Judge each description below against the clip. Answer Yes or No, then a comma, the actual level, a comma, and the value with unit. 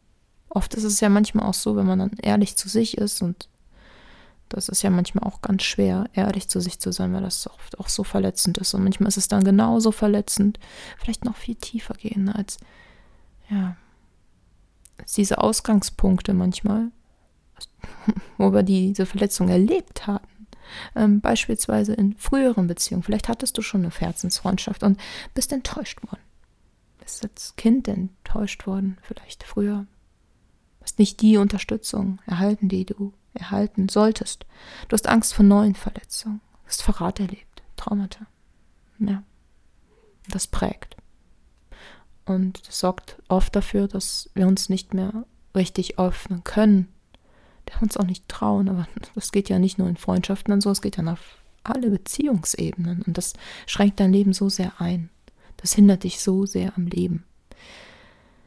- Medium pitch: No, high, 200 Hz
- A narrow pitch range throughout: Yes, narrow, 2.2 semitones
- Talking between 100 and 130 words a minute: No, average, 155 wpm